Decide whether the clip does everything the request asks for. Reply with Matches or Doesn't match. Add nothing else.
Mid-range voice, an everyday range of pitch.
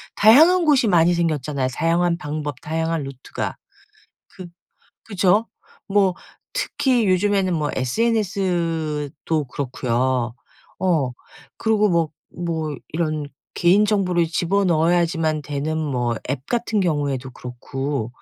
Matches